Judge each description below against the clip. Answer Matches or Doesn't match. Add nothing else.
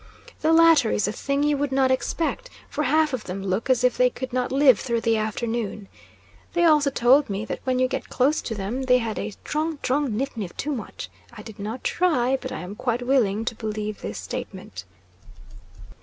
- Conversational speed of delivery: Doesn't match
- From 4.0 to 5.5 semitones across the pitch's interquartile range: Matches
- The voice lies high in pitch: Matches